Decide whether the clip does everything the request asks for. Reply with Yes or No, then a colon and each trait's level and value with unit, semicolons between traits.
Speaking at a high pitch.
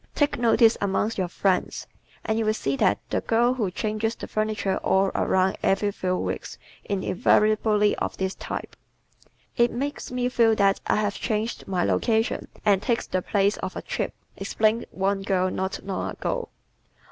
Yes: high, 210 Hz